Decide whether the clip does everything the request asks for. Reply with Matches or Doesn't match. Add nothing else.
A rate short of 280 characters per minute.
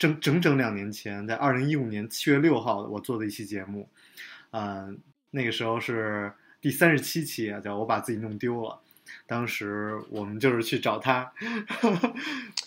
Matches